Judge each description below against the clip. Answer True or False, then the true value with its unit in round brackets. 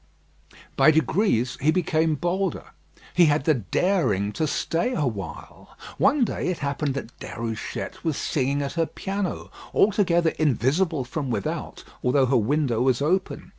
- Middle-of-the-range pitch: True (150 Hz)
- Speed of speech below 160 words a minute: True (140 wpm)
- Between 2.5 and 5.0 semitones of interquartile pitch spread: False (5.4 semitones)